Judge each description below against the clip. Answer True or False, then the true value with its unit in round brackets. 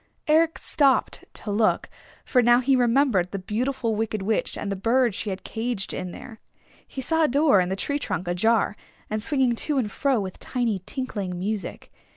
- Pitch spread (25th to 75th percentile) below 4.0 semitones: False (4.8 semitones)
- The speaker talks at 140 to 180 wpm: False (190 wpm)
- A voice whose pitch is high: True (230 Hz)